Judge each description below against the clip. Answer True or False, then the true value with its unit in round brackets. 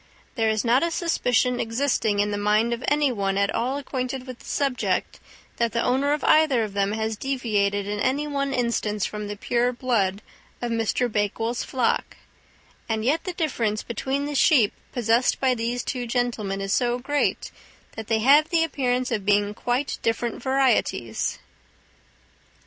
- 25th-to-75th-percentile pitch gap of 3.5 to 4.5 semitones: True (3.8 semitones)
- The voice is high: True (240 Hz)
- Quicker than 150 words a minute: True (170 wpm)